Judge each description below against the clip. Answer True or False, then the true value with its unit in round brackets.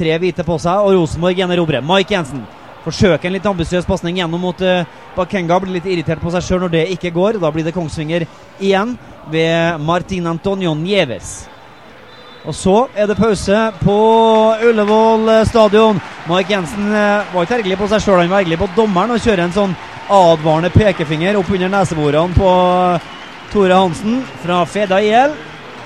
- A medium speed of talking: True (165 wpm)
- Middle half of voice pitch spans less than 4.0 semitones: True (3.4 semitones)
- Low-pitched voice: False (185 Hz)